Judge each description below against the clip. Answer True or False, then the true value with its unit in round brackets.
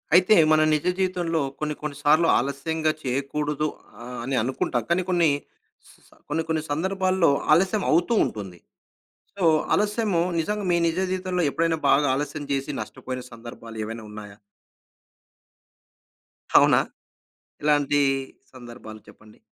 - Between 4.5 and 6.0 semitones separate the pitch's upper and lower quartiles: True (5.2 semitones)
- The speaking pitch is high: False (150 Hz)